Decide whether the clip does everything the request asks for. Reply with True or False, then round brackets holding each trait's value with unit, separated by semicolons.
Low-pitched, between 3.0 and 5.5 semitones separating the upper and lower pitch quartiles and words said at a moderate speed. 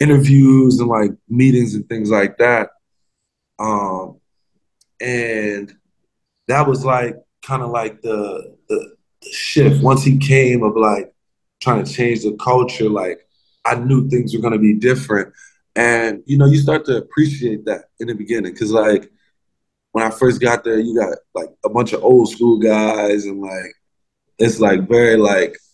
True (120 Hz; 3.6 semitones; 170 wpm)